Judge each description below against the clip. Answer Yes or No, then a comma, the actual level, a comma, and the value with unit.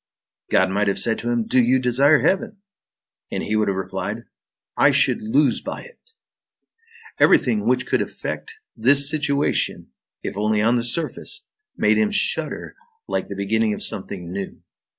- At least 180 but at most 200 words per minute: No, average, 160 wpm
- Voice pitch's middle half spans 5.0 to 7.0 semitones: Yes, wide, 5.4 semitones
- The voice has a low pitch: Yes, low, 120 Hz